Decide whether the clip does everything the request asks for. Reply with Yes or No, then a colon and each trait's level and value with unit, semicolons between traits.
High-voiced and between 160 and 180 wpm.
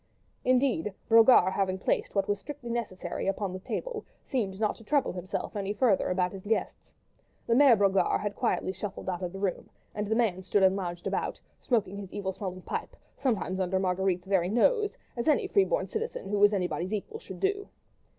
No: high, 200 Hz; average, 195 wpm